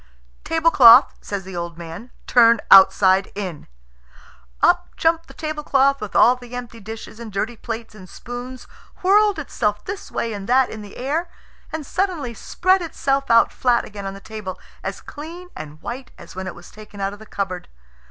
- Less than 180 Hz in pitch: No, high, 230 Hz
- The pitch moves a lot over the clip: Yes, wide, 5.8 semitones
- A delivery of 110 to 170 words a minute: No, average, 180 wpm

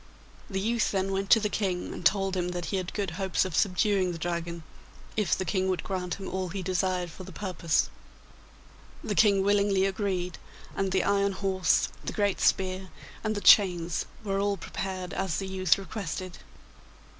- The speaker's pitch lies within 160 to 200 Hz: Yes, high, 190 Hz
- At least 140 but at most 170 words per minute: No, average, 180 wpm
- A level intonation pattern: Yes, narrow, 1.6 semitones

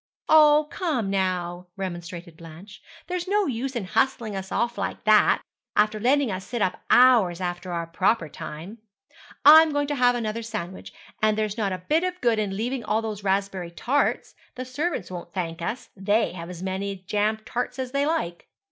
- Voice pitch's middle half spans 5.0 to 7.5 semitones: Yes, wide, 5.5 semitones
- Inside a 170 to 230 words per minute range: Yes, average, 185 wpm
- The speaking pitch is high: Yes, high, 215 Hz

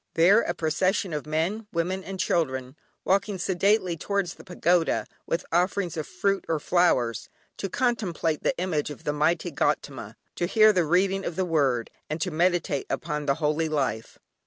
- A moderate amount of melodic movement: Yes, average, 3.7 semitones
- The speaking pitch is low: No, medium, 170 Hz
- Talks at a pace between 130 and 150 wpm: No, average, 170 wpm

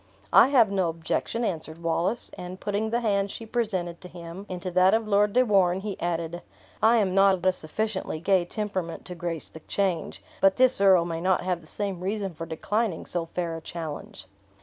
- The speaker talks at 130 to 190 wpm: No, average, 200 wpm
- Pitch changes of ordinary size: Yes, average, 3.4 semitones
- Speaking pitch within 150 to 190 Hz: Yes, medium, 185 Hz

